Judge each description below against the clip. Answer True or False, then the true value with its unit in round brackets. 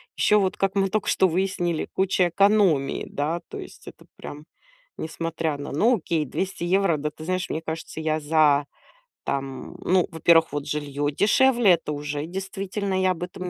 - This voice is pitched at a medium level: True (170 Hz)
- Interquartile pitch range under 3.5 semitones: False (4.1 semitones)